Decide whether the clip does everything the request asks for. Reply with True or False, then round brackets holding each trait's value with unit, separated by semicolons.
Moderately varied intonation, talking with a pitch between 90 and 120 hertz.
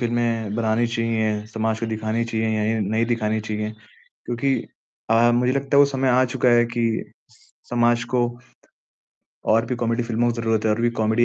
False (1.4 semitones; 115 Hz)